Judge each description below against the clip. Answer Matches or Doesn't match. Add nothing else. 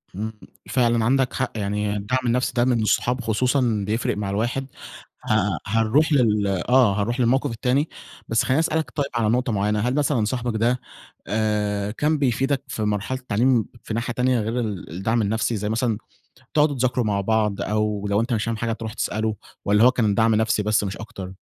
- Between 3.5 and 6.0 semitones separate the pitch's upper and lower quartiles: Doesn't match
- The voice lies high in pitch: Doesn't match